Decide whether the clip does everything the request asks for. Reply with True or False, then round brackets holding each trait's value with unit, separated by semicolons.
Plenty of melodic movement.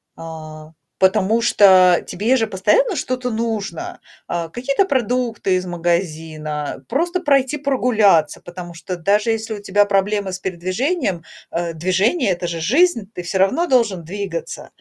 True (5.8 semitones)